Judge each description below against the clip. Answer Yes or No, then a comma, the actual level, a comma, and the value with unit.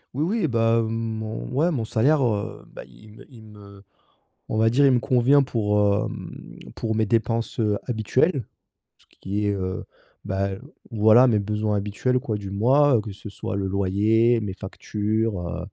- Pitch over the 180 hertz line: No, low, 110 Hz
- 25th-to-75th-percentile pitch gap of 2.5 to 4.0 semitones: Yes, average, 2.9 semitones